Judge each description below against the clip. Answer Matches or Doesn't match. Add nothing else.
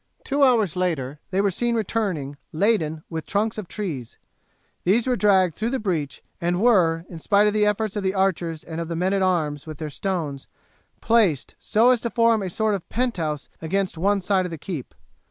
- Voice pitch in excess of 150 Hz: Matches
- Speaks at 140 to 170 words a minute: Doesn't match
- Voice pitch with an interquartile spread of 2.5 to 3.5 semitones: Doesn't match